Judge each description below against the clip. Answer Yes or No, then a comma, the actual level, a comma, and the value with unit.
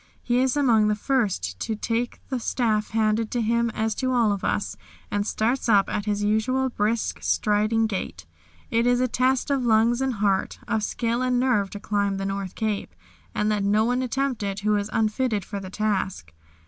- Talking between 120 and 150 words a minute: No, average, 200 wpm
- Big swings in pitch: No, average, 3.0 semitones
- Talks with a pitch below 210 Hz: No, high, 220 Hz